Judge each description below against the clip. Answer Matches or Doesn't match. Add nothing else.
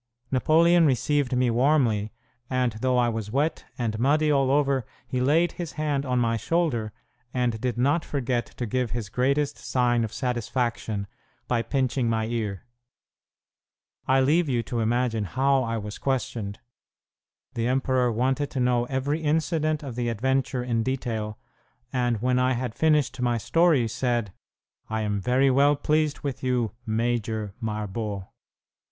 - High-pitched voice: Doesn't match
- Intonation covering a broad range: Doesn't match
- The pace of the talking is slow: Doesn't match